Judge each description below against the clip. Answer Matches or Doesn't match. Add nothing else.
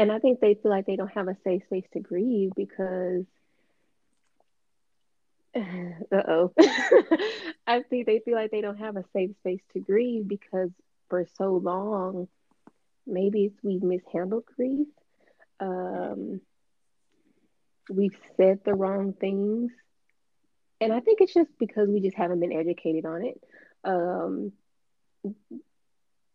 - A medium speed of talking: Doesn't match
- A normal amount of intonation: Matches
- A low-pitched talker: Doesn't match